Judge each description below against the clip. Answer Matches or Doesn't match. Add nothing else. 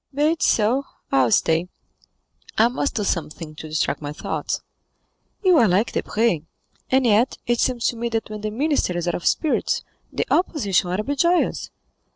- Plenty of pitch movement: Matches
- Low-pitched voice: Doesn't match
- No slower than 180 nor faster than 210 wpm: Matches